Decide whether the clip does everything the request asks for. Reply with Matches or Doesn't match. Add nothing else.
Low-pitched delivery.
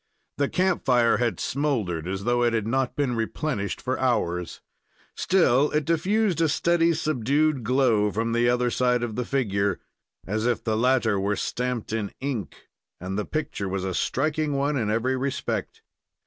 Matches